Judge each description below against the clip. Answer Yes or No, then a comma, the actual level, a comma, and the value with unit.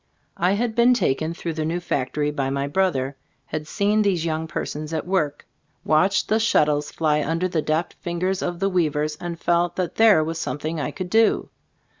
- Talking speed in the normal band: Yes, average, 190 wpm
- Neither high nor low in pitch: Yes, medium, 165 Hz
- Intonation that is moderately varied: Yes, average, 3.5 semitones